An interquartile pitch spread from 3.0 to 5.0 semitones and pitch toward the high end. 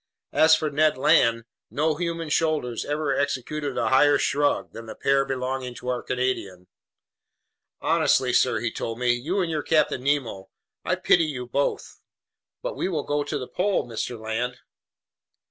No: average, 3.7 semitones; low, 135 Hz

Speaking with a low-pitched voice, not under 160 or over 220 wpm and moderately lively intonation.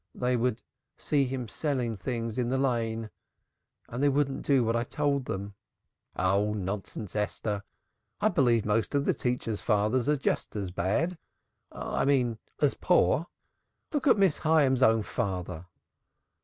No: low, 120 Hz; average, 145 wpm; average, 4.7 semitones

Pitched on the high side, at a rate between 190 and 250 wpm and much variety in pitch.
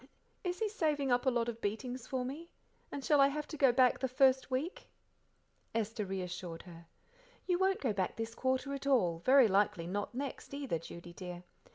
Yes: very high, 255 Hz; average, 195 wpm; wide, 5.9 semitones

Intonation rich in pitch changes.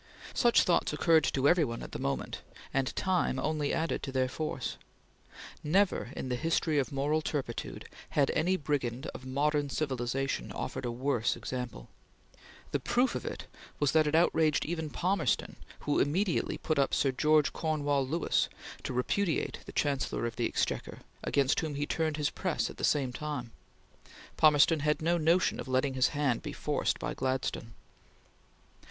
No: average, 3.3 semitones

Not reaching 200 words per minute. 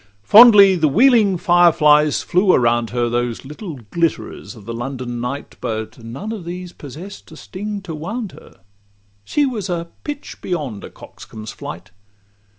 Yes: average, 155 wpm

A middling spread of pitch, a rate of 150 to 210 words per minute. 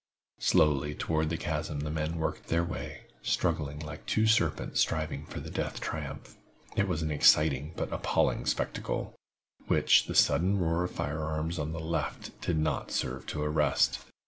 No: narrow, 1.8 semitones; average, 170 wpm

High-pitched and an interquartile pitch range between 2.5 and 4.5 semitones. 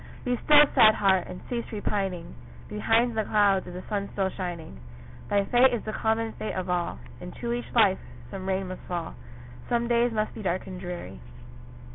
Yes: high, 200 Hz; average, 3.8 semitones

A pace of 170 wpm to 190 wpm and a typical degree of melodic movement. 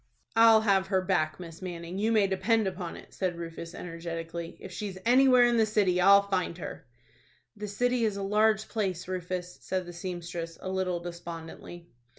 Yes: average, 175 wpm; average, 3.3 semitones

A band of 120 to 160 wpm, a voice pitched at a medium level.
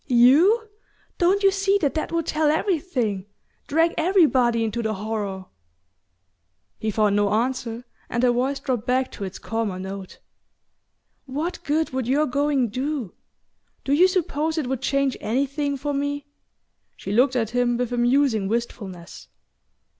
No: average, 150 wpm; very high, 260 Hz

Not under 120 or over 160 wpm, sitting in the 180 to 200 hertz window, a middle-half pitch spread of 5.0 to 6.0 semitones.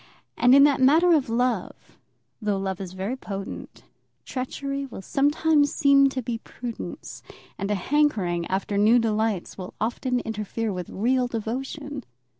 No: average, 145 wpm; high, 235 Hz; average, 5.3 semitones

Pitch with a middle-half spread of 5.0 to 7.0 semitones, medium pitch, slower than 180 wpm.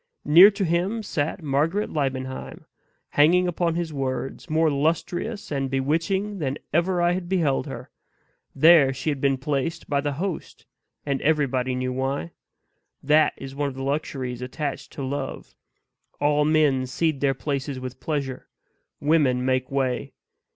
No: average, 3.5 semitones; medium, 145 Hz; average, 150 wpm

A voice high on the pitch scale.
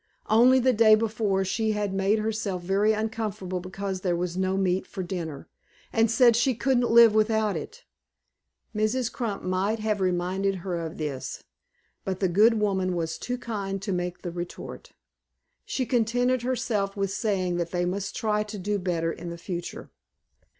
Yes: high, 200 Hz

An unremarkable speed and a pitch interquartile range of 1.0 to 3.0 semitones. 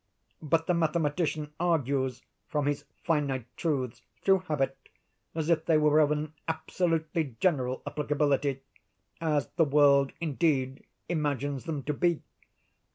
No: slow, 120 wpm; narrow, 2.6 semitones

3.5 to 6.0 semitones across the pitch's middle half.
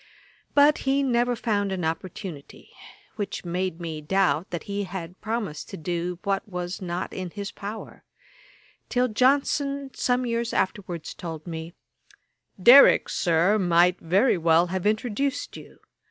Yes: average, 5.3 semitones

